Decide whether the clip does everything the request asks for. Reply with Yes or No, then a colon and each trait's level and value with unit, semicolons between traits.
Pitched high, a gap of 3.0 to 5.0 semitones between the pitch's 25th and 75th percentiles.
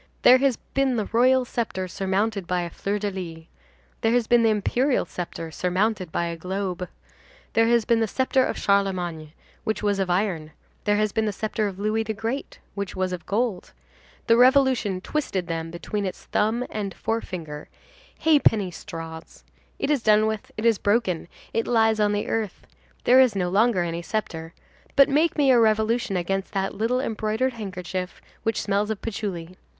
Yes: high, 210 Hz; average, 3.9 semitones